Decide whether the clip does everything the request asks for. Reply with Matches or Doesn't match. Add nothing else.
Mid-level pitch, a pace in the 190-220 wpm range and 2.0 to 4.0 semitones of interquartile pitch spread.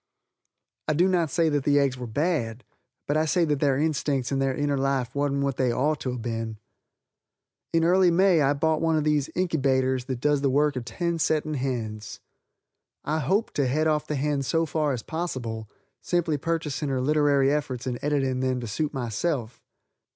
Matches